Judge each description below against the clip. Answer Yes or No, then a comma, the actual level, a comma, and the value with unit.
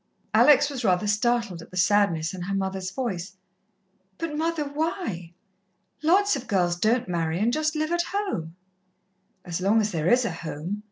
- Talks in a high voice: Yes, high, 205 Hz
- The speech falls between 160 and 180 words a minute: Yes, average, 170 wpm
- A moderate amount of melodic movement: No, wide, 8.6 semitones